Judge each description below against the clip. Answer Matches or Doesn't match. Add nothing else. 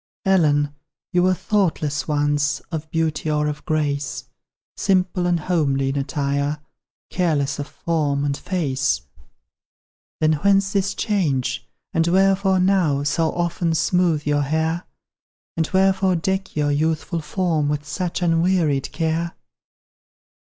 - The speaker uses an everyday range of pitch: Matches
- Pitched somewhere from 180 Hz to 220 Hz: Doesn't match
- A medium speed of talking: Doesn't match